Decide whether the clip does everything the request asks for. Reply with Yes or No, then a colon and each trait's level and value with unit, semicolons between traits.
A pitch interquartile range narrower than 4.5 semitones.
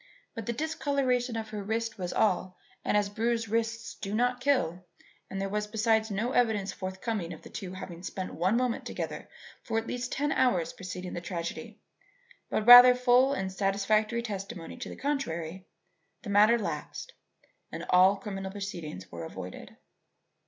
Yes: average, 3.9 semitones